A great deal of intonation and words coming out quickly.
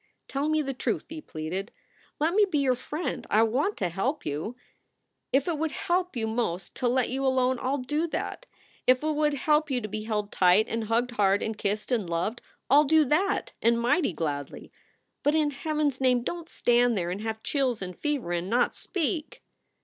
Yes: wide, 5.8 semitones; fast, 210 wpm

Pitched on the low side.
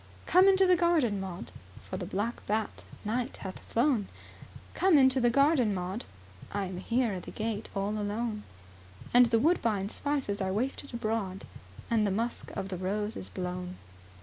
No: high, 215 Hz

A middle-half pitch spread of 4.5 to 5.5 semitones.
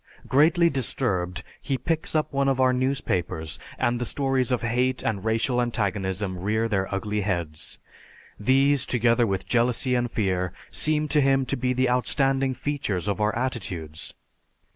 Yes: average, 5.1 semitones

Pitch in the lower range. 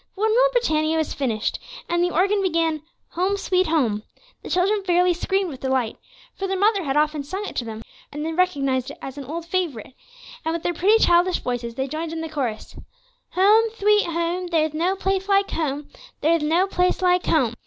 No: very high, 335 Hz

